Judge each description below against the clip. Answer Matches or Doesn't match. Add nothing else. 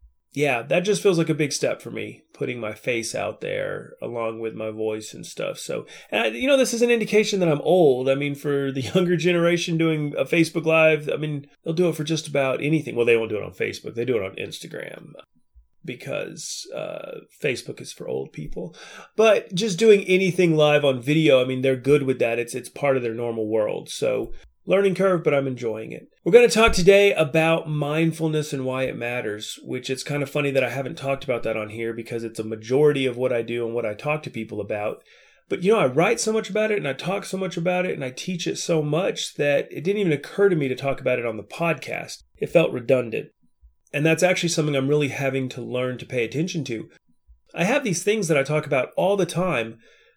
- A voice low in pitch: Doesn't match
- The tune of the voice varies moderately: Doesn't match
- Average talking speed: Doesn't match